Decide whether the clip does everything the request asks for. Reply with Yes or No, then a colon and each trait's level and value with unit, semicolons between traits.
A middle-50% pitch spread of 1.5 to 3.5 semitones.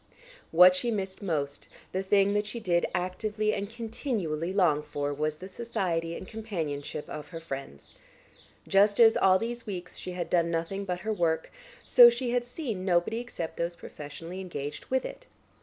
No: average, 4.6 semitones